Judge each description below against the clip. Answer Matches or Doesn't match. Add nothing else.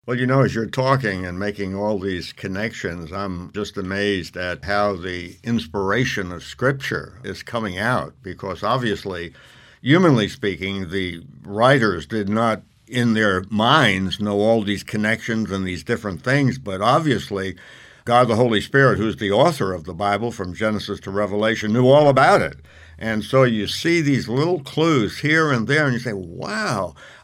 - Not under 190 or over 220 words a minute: Doesn't match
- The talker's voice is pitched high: Doesn't match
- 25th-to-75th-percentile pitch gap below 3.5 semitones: Doesn't match